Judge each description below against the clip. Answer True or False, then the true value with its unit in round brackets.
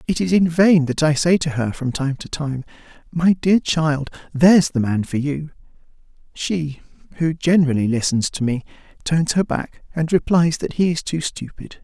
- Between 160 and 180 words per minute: False (190 wpm)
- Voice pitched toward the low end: False (155 Hz)